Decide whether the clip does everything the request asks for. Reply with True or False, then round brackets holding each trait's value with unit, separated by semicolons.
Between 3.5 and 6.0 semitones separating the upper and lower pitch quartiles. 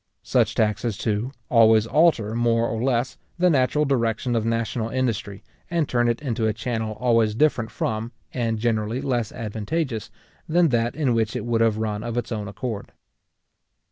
False (2.4 semitones)